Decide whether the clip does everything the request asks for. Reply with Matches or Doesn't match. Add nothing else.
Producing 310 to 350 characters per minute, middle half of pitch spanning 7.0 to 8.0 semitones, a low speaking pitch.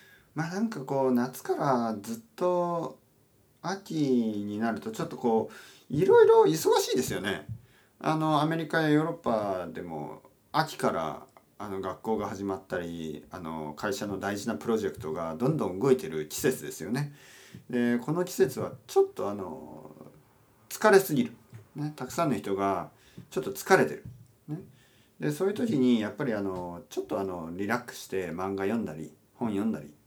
Matches